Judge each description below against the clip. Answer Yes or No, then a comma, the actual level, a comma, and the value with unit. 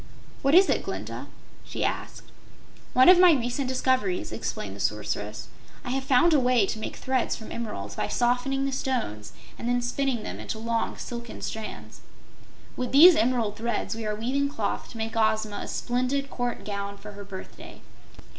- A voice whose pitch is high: Yes, high, 245 Hz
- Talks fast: No, average, 175 wpm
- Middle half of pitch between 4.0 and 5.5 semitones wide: No, average, 3.6 semitones